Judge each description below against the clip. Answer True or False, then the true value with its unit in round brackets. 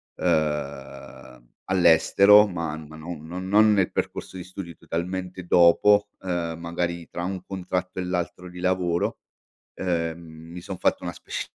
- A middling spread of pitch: False (1.9 semitones)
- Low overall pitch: True (90 Hz)